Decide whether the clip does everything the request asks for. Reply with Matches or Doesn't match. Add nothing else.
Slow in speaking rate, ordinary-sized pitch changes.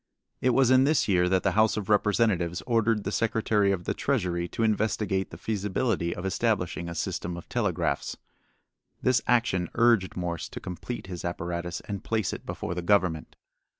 Doesn't match